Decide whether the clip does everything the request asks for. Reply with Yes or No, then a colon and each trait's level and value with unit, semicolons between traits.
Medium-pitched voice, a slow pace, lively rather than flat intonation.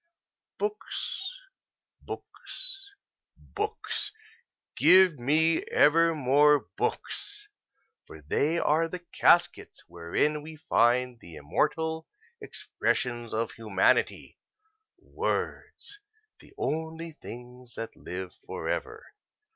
Yes: medium, 155 Hz; slow, 85 wpm; wide, 5.8 semitones